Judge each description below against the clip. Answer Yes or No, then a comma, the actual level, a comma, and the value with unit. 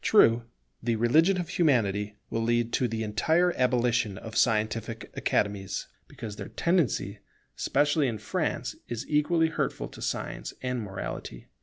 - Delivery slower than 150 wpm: Yes, average, 140 wpm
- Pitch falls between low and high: No, low, 115 Hz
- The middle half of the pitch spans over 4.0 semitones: Yes, wide, 5.4 semitones